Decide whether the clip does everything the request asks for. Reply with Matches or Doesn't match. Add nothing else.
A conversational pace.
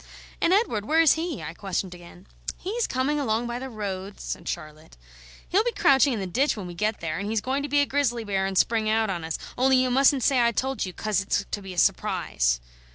Doesn't match